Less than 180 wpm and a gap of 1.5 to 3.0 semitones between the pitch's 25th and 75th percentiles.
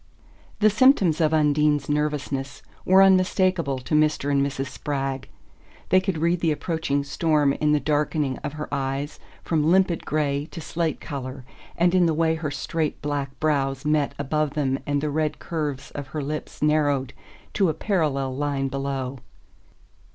Yes: average, 160 wpm; narrow, 2.5 semitones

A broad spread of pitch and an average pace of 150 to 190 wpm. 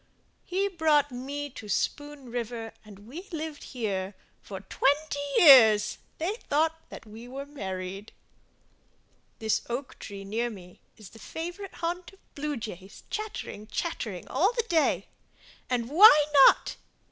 No: wide, 6.9 semitones; slow, 135 wpm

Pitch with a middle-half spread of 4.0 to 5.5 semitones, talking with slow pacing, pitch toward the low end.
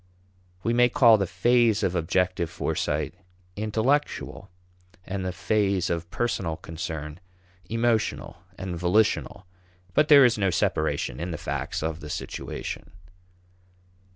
Yes: average, 5.1 semitones; slow, 125 wpm; very low, 95 Hz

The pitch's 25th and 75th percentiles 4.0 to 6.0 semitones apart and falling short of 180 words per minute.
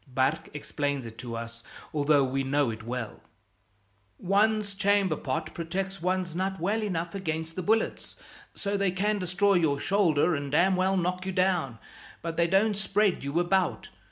Yes: average, 5.2 semitones; average, 165 wpm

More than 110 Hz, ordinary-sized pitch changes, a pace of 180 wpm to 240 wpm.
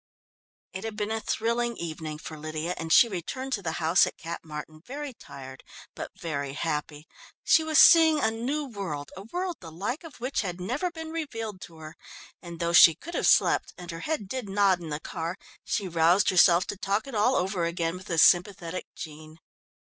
No: medium, 185 Hz; wide, 6.2 semitones; average, 200 wpm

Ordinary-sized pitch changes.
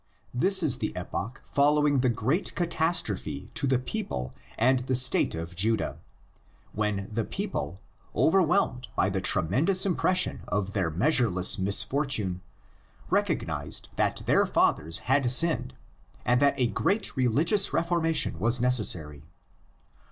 No: wide, 8.0 semitones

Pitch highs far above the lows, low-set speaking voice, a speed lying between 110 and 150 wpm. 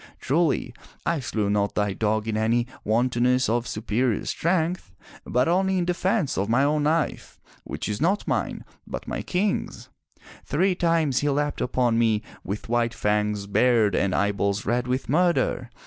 No: wide, 6.8 semitones; low, 125 Hz; average, 160 wpm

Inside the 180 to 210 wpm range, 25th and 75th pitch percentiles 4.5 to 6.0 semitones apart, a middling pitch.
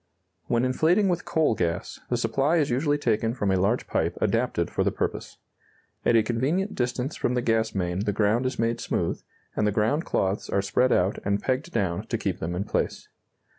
No: fast, 205 wpm; average, 4.8 semitones; low, 115 Hz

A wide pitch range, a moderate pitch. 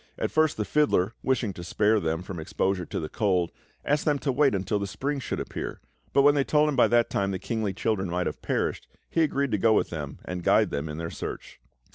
No: wide, 7.5 semitones; low, 105 Hz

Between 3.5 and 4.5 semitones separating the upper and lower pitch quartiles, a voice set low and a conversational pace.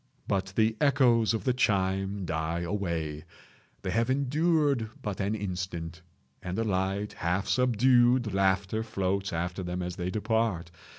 No: average, 4.2 semitones; low, 100 Hz; slow, 130 wpm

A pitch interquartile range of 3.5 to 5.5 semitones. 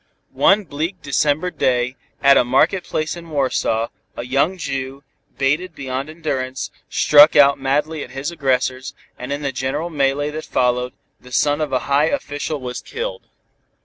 No: average, 3.0 semitones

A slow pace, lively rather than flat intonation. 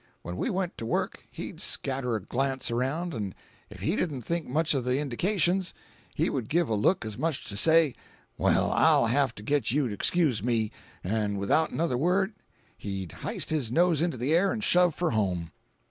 No: average, 200 wpm; wide, 7.0 semitones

